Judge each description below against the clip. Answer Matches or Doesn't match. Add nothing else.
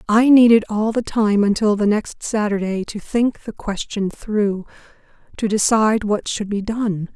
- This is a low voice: Doesn't match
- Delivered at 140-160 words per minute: Doesn't match